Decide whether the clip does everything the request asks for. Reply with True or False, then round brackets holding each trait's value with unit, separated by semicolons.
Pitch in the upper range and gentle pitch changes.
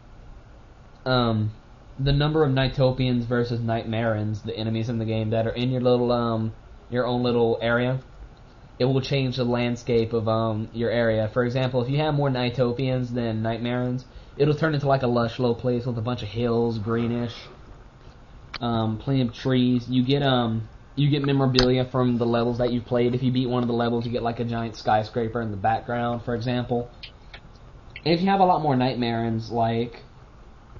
False (120 Hz; 1.7 semitones)